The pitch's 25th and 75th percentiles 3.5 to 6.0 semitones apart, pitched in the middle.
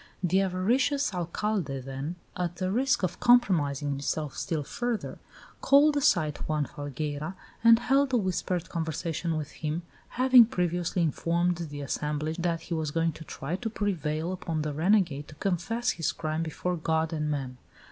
Yes: average, 4.2 semitones; medium, 170 Hz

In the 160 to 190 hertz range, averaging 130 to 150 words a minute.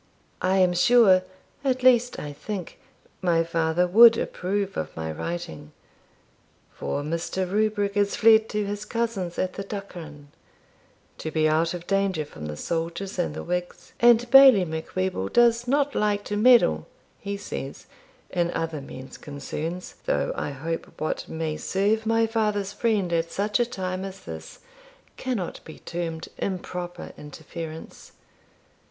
Yes: medium, 185 Hz; average, 145 wpm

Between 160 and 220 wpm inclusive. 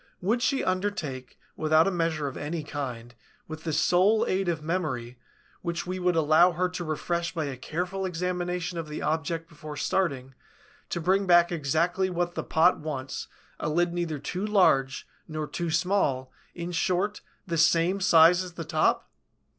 Yes: average, 170 wpm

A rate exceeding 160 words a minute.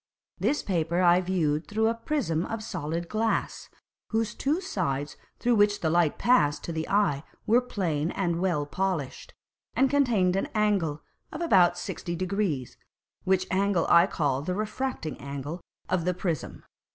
No: average, 155 wpm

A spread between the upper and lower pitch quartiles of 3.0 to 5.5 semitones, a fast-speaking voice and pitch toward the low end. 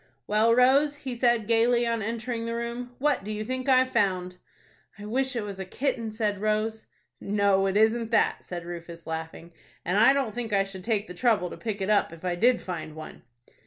No: average, 3.8 semitones; fast, 210 wpm; high, 220 Hz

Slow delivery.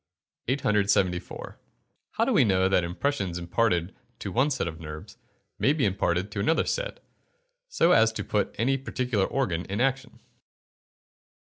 No: average, 145 wpm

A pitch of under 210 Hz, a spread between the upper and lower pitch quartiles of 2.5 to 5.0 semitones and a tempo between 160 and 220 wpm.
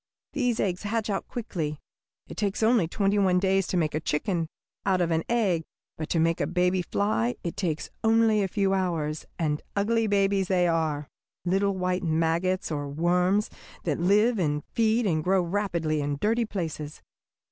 Yes: medium, 185 Hz; average, 3.9 semitones; average, 175 wpm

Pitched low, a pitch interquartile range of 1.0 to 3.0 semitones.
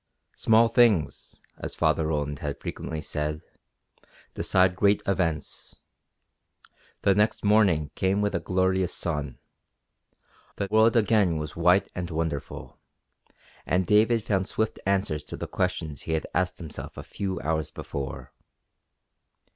No: very low, 90 Hz; average, 4.4 semitones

